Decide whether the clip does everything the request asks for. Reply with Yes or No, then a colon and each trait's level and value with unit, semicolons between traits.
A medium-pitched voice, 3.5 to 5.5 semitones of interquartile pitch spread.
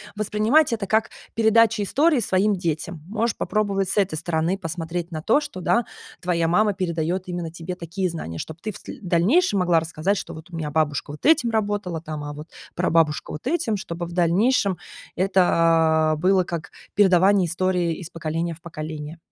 Yes: medium, 180 Hz; average, 3.9 semitones